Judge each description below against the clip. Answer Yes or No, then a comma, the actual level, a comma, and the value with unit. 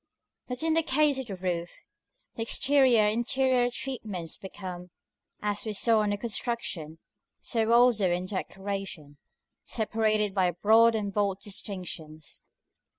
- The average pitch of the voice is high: Yes, high, 210 Hz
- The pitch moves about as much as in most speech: Yes, average, 4.2 semitones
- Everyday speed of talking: No, slow, 130 wpm